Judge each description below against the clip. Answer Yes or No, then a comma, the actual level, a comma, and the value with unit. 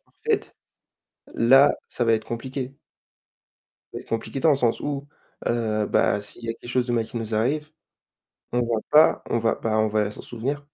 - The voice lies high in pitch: No, low, 120 Hz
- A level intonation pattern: No, average, 3.2 semitones